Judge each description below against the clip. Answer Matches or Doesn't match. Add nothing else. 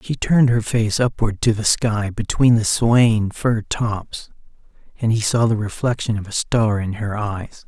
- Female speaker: Doesn't match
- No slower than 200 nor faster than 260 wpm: Doesn't match